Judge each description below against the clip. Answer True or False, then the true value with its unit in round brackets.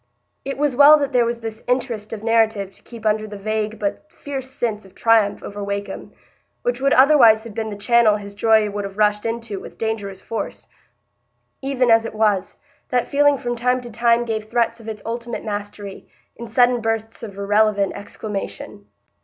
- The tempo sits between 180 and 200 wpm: True (185 wpm)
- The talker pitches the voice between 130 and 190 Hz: False (225 Hz)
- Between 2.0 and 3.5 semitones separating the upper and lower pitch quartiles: True (2.5 semitones)